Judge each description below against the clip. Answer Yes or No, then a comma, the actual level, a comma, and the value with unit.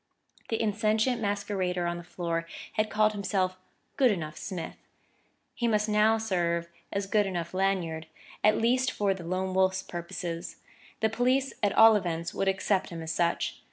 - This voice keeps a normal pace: Yes, average, 160 wpm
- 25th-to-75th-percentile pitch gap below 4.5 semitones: Yes, average, 3.8 semitones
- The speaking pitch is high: Yes, high, 195 Hz